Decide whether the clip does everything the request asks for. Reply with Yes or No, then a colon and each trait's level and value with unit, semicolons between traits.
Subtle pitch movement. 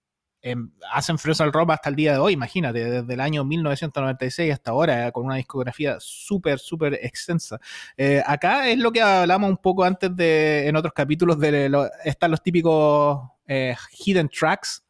No: average, 3.9 semitones